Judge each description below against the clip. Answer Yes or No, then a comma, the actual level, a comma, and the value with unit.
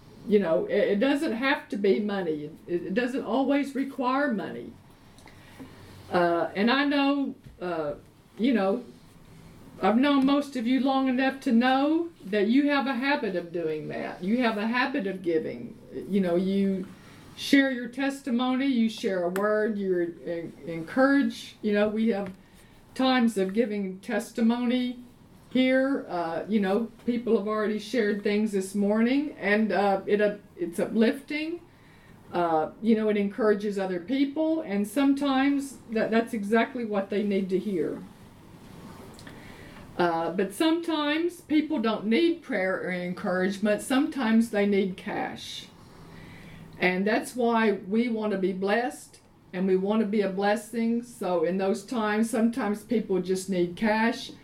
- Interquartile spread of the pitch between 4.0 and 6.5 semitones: Yes, average, 5.1 semitones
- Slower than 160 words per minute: Yes, average, 150 wpm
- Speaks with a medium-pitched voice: No, high, 215 Hz